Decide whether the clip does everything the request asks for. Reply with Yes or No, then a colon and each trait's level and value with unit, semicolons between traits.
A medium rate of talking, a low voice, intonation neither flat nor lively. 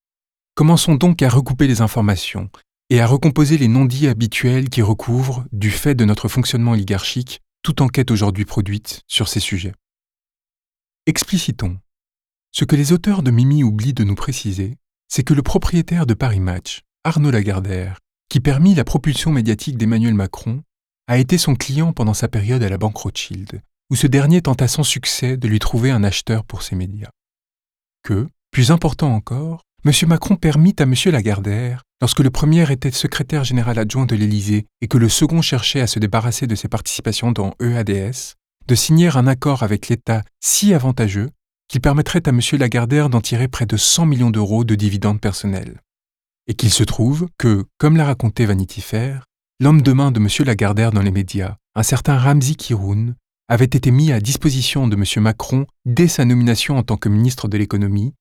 Yes: average, 180 wpm; low, 120 Hz; average, 4.8 semitones